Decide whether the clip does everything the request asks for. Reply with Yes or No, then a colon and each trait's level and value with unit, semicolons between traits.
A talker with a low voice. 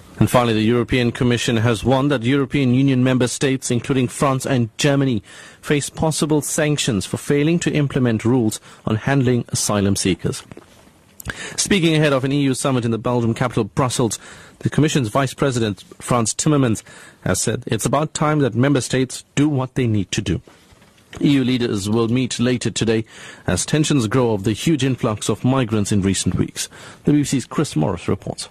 Yes: low, 125 Hz